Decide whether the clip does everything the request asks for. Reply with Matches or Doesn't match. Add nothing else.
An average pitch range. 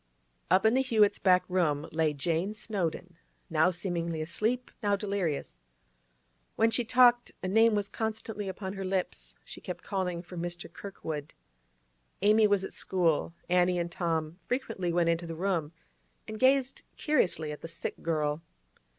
Matches